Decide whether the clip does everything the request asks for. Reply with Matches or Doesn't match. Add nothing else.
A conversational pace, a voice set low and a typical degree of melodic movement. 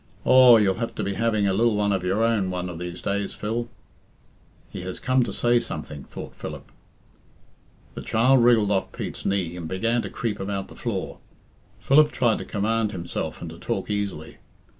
Matches